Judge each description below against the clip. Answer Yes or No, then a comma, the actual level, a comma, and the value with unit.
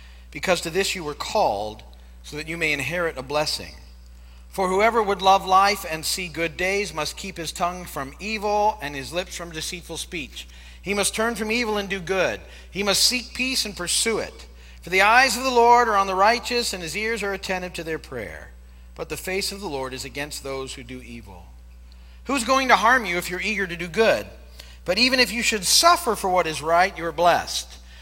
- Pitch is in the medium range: Yes, medium, 175 Hz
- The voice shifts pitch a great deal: Yes, wide, 7.7 semitones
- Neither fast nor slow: No, fast, 220 wpm